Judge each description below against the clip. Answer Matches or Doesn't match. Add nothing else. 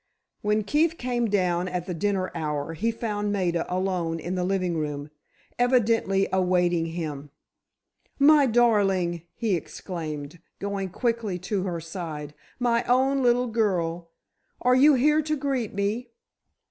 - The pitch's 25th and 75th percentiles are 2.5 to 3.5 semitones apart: Doesn't match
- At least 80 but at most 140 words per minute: Matches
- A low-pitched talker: Doesn't match